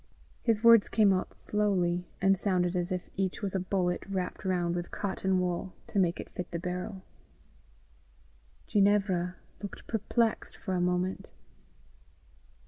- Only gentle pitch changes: Yes, narrow, 2.0 semitones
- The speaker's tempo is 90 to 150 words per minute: Yes, average, 140 wpm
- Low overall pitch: No, medium, 185 Hz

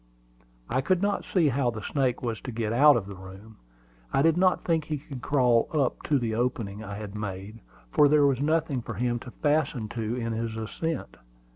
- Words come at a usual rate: No, fast, 210 wpm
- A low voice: Yes, low, 125 Hz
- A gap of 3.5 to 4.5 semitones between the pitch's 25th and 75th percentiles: No, average, 4.9 semitones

